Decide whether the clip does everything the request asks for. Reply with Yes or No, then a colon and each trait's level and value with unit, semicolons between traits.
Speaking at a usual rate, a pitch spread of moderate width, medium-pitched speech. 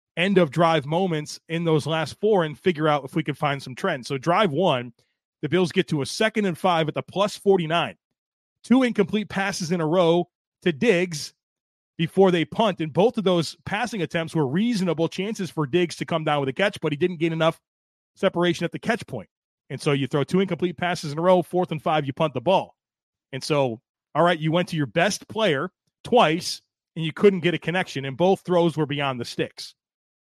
No: fast, 220 wpm; average, 3.5 semitones; medium, 170 Hz